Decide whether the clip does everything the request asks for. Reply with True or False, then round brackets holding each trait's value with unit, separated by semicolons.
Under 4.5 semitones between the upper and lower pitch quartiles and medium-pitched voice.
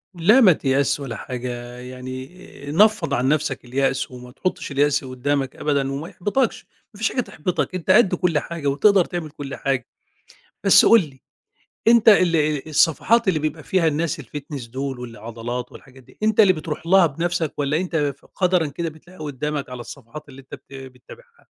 False (4.8 semitones; 150 Hz)